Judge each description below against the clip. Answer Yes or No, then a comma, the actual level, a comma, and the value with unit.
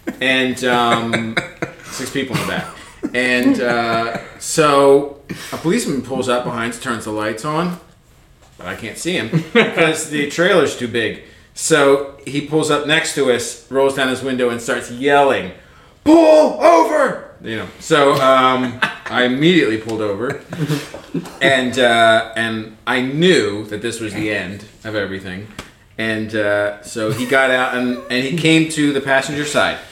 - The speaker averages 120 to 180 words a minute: Yes, average, 160 wpm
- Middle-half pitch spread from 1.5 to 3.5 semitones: No, average, 4.3 semitones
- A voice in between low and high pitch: No, low, 130 Hz